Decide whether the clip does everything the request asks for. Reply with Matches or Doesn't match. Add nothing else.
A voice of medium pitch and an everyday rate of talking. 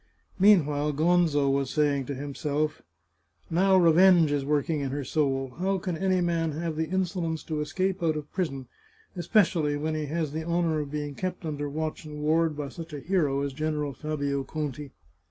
Matches